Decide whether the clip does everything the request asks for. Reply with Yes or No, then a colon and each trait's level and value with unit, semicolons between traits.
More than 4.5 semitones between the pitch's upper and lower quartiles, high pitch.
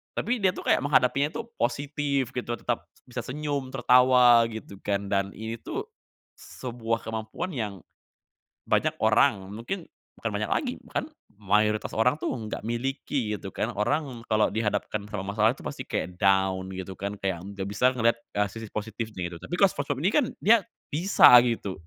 No: average, 4.9 semitones; low, 115 Hz